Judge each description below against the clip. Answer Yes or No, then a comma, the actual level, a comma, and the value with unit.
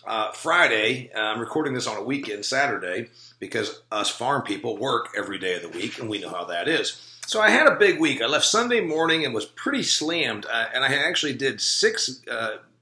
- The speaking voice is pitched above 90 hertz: Yes, medium, 140 Hz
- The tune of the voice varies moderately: No, wide, 8.2 semitones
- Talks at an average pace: No, fast, 220 wpm